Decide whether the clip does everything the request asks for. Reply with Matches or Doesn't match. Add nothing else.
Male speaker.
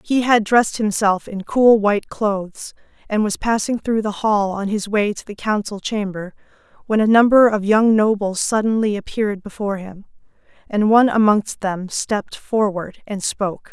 Doesn't match